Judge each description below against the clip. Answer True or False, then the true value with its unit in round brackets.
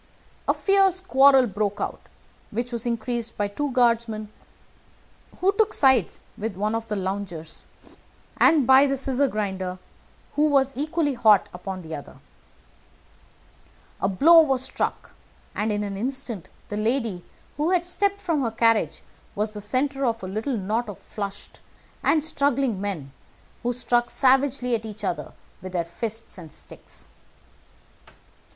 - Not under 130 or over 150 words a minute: True (145 wpm)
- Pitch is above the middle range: True (230 Hz)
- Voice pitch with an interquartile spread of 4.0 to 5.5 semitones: True (5.0 semitones)